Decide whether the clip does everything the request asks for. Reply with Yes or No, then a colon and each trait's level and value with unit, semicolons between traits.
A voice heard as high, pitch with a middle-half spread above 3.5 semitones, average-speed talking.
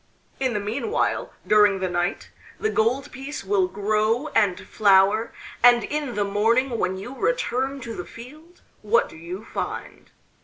Yes: high, 225 Hz; average, 4.8 semitones; average, 155 wpm